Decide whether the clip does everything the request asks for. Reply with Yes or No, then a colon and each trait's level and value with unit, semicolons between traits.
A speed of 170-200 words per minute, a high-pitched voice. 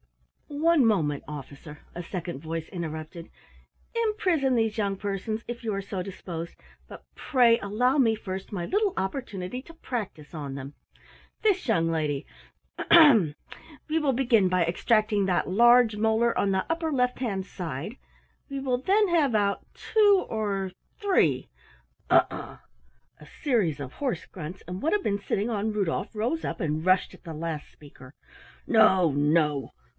No: average, 160 wpm; high, 205 Hz